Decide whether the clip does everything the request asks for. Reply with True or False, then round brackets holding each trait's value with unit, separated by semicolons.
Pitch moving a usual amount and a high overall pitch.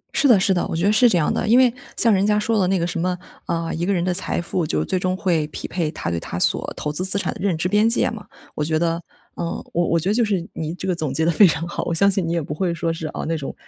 False (3.2 semitones; 175 Hz)